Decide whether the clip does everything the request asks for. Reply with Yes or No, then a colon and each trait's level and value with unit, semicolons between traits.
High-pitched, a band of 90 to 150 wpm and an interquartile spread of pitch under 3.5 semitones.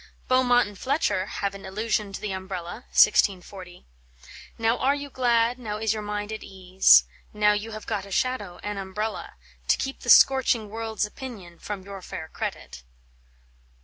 No: high, 210 Hz; average, 165 wpm; average, 3.0 semitones